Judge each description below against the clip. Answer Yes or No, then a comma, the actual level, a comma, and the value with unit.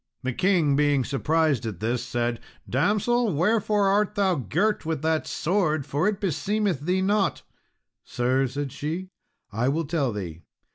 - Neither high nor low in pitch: Yes, medium, 155 Hz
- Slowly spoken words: No, average, 150 wpm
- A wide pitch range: Yes, wide, 6.8 semitones